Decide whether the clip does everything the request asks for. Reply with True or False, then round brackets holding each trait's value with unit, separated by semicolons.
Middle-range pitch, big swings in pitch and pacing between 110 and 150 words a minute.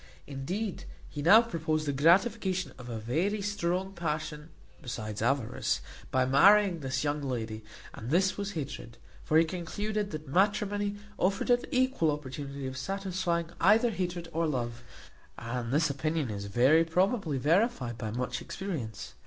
True (160 Hz; 6.6 semitones; 145 wpm)